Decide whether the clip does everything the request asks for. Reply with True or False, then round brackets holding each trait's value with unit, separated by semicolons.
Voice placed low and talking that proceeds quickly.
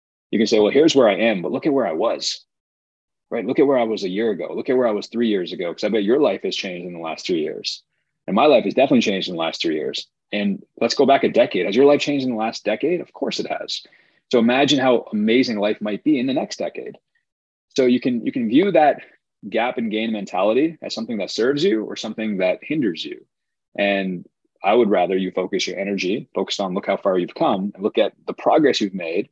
True (115 Hz; 260 wpm)